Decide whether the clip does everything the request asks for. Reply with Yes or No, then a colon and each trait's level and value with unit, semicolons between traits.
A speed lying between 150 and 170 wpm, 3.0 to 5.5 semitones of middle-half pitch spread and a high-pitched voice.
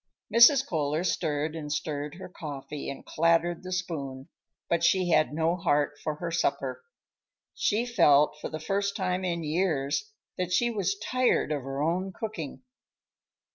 No: average, 155 wpm; average, 4.0 semitones; medium, 165 Hz